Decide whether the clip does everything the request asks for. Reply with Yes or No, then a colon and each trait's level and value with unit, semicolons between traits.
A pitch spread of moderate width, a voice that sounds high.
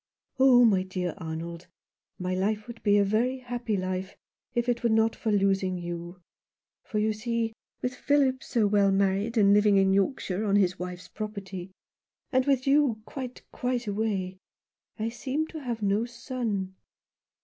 Yes: average, 4.1 semitones; high, 210 Hz